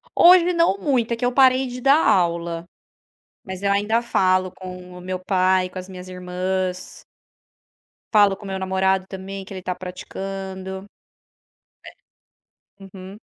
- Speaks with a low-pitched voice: No, high, 190 Hz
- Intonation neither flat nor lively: No, narrow, 1.9 semitones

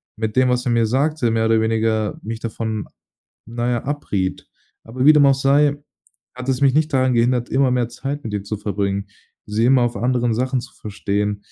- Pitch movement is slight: No, average, 3.0 semitones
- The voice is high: No, low, 120 Hz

